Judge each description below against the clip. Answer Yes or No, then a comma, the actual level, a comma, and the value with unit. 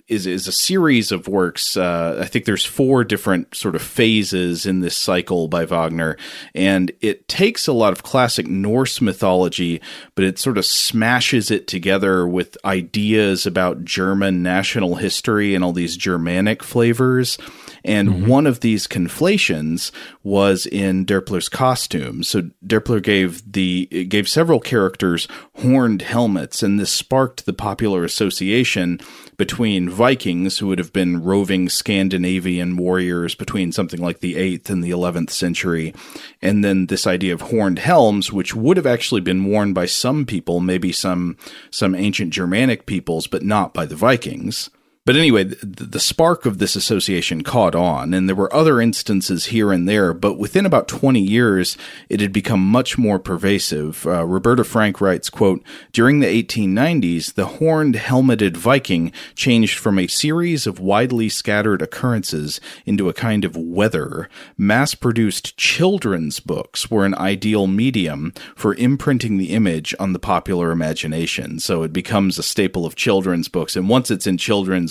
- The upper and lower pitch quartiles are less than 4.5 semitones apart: Yes, average, 3.9 semitones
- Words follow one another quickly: No, average, 160 wpm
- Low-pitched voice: Yes, very low, 95 Hz